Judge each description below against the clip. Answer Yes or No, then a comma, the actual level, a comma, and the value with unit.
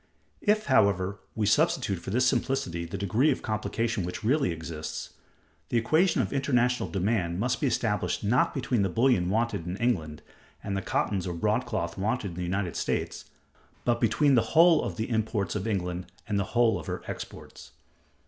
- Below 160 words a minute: No, average, 175 wpm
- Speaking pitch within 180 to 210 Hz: No, low, 110 Hz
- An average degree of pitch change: Yes, average, 5.0 semitones